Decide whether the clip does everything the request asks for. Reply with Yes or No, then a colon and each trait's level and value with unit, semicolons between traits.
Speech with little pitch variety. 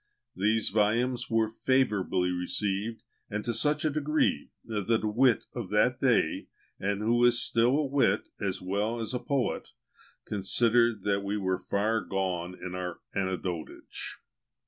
No: average, 3.6 semitones